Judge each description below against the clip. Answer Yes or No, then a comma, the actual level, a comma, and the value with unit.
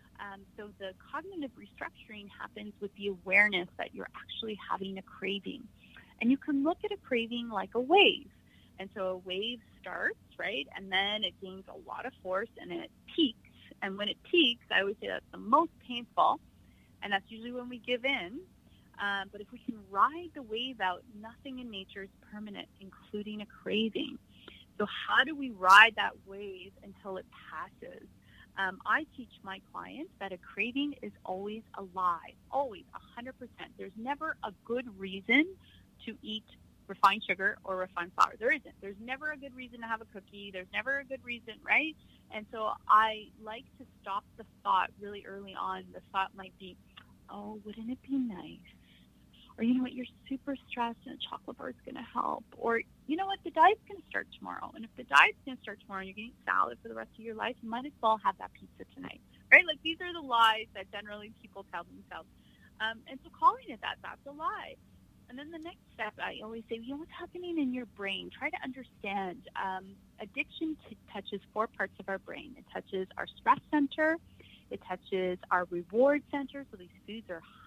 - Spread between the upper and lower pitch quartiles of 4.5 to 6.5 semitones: Yes, average, 5.3 semitones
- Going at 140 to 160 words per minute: No, fast, 205 wpm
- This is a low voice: No, high, 220 Hz